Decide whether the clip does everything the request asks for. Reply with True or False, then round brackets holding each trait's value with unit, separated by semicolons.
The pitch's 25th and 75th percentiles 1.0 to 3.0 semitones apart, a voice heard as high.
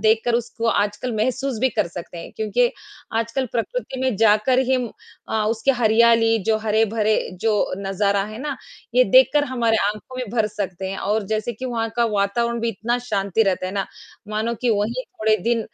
True (2.4 semitones; 225 Hz)